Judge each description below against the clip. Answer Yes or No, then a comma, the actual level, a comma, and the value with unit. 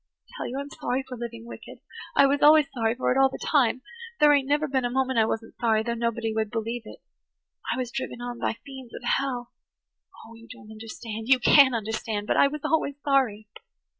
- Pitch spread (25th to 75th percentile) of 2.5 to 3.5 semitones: Yes, average, 3.1 semitones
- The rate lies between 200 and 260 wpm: Yes, fast, 205 wpm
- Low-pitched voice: No, high, 245 Hz